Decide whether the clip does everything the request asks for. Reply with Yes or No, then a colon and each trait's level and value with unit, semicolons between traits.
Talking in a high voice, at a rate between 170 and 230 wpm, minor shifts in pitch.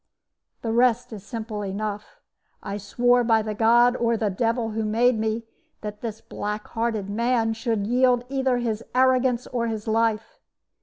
No: high, 225 Hz; average, 160 wpm; narrow, 2.3 semitones